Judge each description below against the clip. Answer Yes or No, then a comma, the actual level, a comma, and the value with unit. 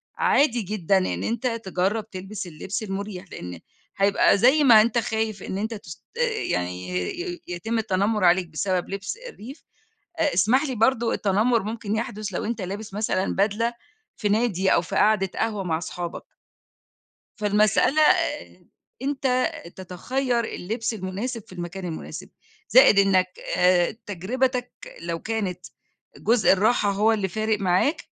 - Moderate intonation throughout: Yes, average, 3.7 semitones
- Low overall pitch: No, high, 210 Hz